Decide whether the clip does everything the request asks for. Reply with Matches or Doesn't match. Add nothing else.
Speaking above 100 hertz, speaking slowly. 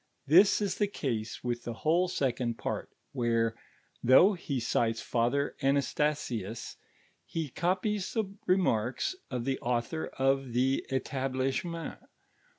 Matches